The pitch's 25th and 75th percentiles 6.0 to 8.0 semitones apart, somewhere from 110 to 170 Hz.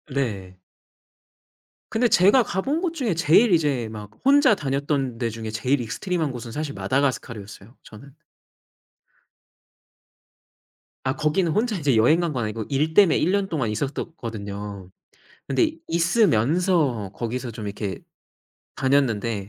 Yes: wide, 7.5 semitones; medium, 140 Hz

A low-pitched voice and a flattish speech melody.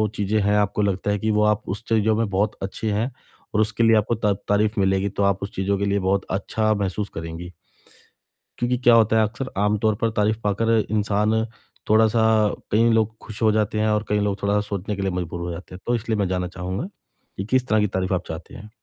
Yes: low, 105 Hz; narrow, 1.9 semitones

